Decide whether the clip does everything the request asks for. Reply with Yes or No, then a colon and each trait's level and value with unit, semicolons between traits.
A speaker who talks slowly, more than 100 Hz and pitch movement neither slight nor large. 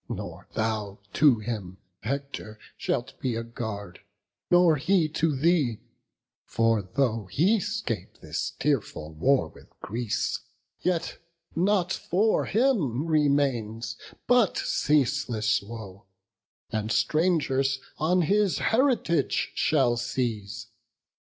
No: slow, 105 wpm; low, 135 Hz; wide, 6.9 semitones